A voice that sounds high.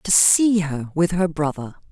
No: medium, 165 Hz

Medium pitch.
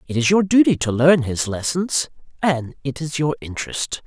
Yes: medium, 145 Hz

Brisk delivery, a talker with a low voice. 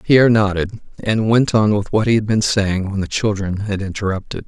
Yes: fast, 215 wpm; low, 105 Hz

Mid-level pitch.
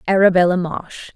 Yes: medium, 180 Hz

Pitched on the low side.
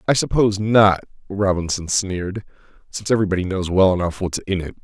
Yes: very low, 95 Hz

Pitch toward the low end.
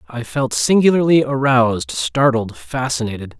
Yes: low, 130 Hz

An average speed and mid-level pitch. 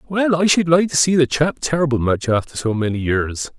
No: fast, 235 wpm; medium, 145 Hz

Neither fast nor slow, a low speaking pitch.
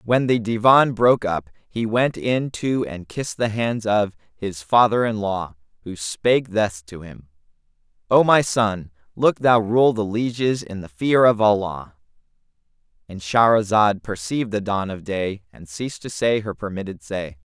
Yes: average, 170 wpm; low, 105 Hz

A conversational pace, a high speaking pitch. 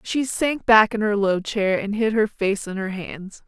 No: fast, 240 wpm; high, 205 Hz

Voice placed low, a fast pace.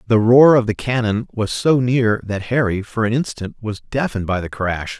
Yes: low, 115 Hz; fast, 215 wpm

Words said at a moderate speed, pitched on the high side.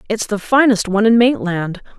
Yes: average, 180 wpm; high, 210 Hz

